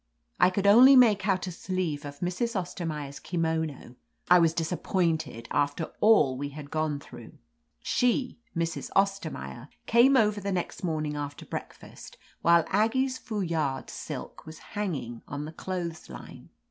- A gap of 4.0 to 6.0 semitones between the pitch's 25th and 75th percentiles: Yes, average, 5.1 semitones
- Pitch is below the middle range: No, medium, 170 Hz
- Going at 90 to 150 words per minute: Yes, average, 145 wpm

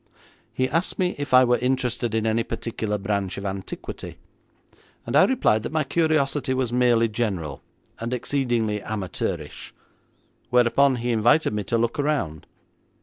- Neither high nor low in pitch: No, low, 120 Hz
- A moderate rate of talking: Yes, average, 145 wpm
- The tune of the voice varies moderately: Yes, average, 3.7 semitones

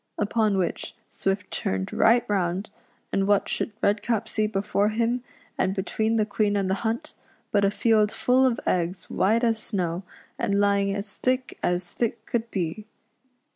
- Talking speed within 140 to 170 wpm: Yes, average, 165 wpm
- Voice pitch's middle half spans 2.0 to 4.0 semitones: Yes, average, 2.7 semitones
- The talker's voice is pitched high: Yes, high, 205 Hz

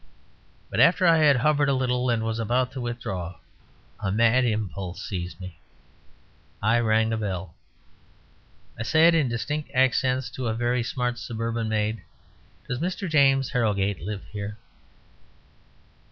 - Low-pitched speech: Yes, low, 120 Hz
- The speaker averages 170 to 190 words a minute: No, average, 140 wpm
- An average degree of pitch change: Yes, average, 3.5 semitones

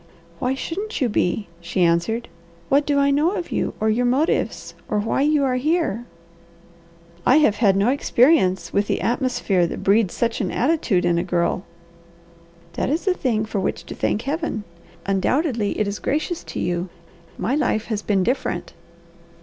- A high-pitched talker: Yes, high, 230 Hz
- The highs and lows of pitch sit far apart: Yes, wide, 6.4 semitones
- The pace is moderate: Yes, average, 175 wpm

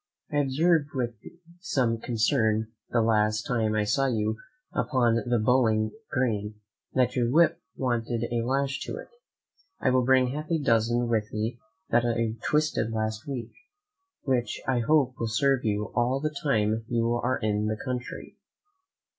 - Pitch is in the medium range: No, low, 120 Hz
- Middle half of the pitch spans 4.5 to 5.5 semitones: No, average, 3.1 semitones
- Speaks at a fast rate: No, average, 155 wpm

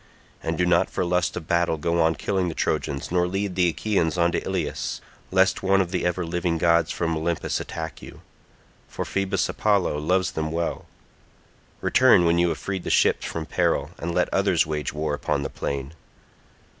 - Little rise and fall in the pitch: Yes, narrow, 2.3 semitones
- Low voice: Yes, very low, 85 Hz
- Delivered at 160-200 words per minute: Yes, average, 185 wpm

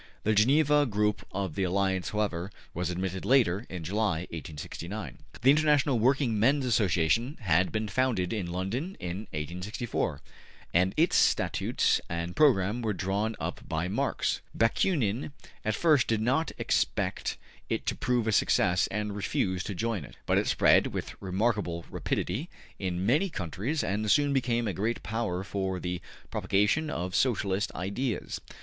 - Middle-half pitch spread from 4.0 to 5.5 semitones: Yes, average, 4.9 semitones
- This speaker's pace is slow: No, average, 150 wpm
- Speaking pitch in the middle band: No, low, 105 Hz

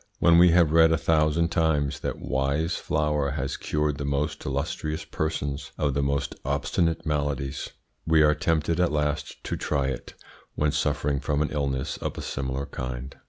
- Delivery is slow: No, average, 170 wpm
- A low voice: Yes, very low, 75 Hz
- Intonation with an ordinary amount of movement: No, narrow, 1.9 semitones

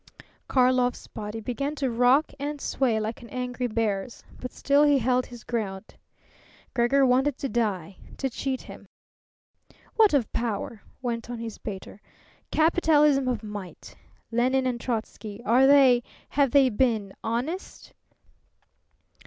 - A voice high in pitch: Yes, high, 245 Hz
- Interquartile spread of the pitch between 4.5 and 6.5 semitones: No, average, 3.3 semitones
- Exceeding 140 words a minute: No, slow, 135 wpm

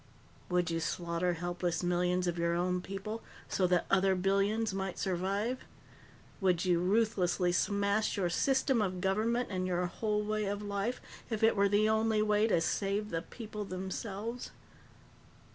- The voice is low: No, high, 195 Hz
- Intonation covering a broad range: No, average, 3.0 semitones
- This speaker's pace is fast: No, average, 155 wpm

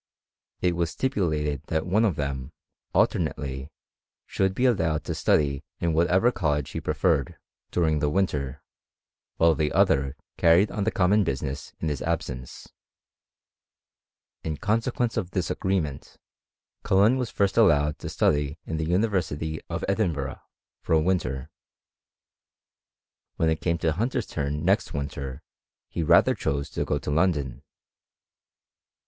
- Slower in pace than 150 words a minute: Yes, average, 140 wpm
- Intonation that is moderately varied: Yes, average, 4.5 semitones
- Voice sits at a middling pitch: No, very low, 80 Hz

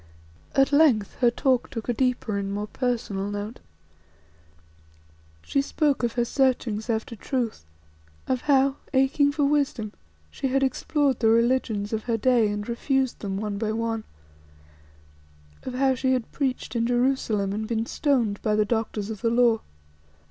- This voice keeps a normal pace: Yes, average, 155 wpm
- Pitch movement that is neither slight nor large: Yes, average, 3.5 semitones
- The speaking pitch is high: Yes, high, 235 Hz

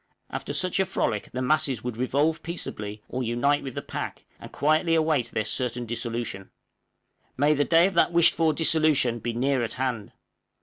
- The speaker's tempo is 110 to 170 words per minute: No, average, 180 wpm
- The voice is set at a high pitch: No, low, 135 Hz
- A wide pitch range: No, average, 4.9 semitones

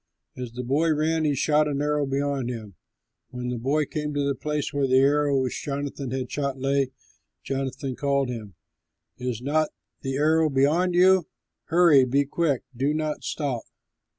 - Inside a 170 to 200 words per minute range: Yes, average, 175 wpm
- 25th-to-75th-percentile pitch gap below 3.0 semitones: Yes, narrow, 2.4 semitones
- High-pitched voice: No, medium, 140 Hz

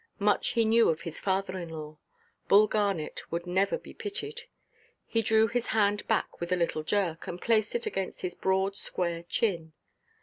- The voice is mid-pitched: No, high, 195 Hz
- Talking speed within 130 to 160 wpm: No, average, 170 wpm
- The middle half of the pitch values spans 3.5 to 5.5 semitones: Yes, average, 4.2 semitones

